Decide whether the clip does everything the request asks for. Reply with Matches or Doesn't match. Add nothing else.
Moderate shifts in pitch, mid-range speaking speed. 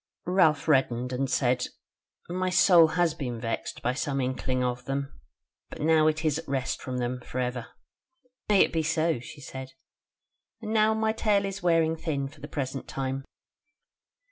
Matches